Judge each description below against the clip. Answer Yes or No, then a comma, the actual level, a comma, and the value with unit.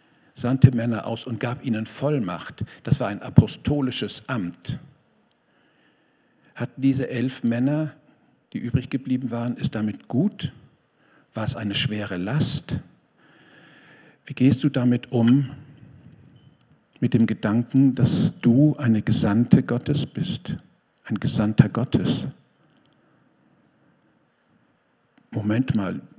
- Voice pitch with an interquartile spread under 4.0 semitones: Yes, average, 2.9 semitones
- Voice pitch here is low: Yes, low, 125 Hz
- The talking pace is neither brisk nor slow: No, slow, 110 wpm